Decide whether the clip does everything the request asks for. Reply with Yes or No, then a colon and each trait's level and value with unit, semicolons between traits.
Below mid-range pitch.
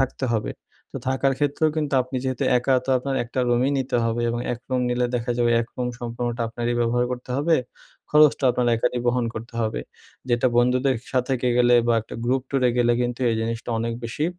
Yes: low, 125 Hz